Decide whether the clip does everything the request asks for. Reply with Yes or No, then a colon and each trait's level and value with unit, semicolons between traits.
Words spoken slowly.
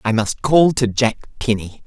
No: average, 195 wpm